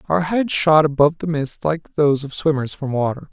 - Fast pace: Yes, fast, 215 wpm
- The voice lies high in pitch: No, medium, 145 Hz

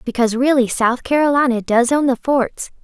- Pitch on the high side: Yes, very high, 255 Hz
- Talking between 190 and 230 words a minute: No, average, 170 wpm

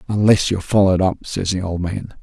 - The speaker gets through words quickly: Yes, fast, 215 wpm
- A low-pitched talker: Yes, very low, 95 Hz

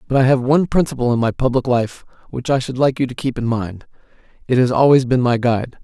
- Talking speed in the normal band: No, fast, 245 wpm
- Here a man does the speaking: Yes, male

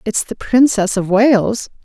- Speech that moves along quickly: No, average, 165 wpm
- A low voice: No, high, 220 Hz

